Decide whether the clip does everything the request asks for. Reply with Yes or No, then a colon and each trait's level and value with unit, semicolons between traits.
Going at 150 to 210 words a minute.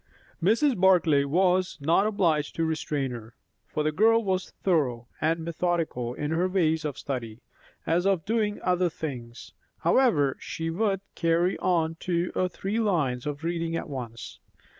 Yes: average, 155 wpm